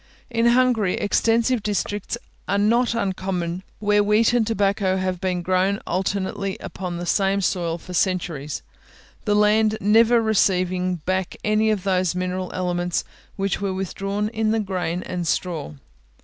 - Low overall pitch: No, high, 195 Hz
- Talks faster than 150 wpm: No, average, 145 wpm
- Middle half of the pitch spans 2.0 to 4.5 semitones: Yes, average, 2.7 semitones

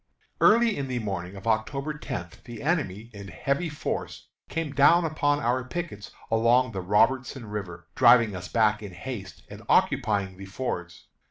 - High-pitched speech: No, low, 115 Hz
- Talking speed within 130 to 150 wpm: No, average, 160 wpm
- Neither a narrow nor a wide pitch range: No, wide, 6.0 semitones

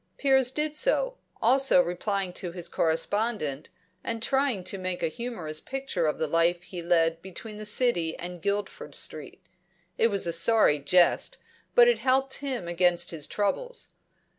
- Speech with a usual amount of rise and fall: No, wide, 7.0 semitones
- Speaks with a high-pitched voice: Yes, high, 195 Hz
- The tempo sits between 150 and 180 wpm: Yes, average, 160 wpm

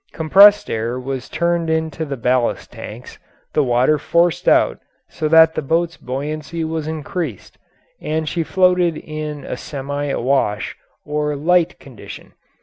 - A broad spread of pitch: No, average, 3.2 semitones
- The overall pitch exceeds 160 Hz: No, medium, 155 Hz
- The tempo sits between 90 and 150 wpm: Yes, average, 140 wpm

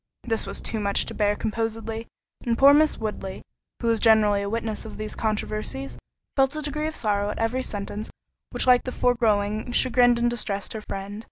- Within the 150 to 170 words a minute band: No, average, 185 wpm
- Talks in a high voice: Yes, high, 220 Hz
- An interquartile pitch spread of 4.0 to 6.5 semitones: No, average, 2.7 semitones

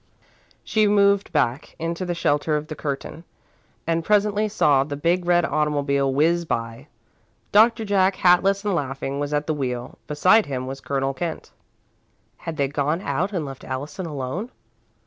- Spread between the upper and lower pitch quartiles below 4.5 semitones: No, average, 4.9 semitones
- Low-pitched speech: No, medium, 155 Hz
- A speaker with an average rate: Yes, average, 160 wpm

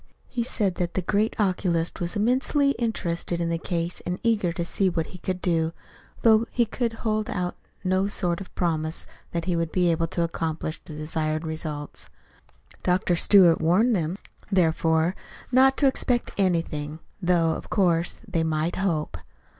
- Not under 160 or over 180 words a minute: Yes, average, 165 wpm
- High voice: No, medium, 175 Hz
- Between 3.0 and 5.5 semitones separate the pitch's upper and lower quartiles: Yes, average, 3.5 semitones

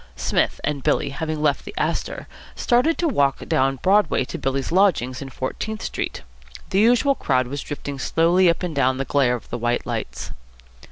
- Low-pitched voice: No, medium, 145 Hz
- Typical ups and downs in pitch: No, wide, 6.0 semitones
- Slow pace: No, average, 185 wpm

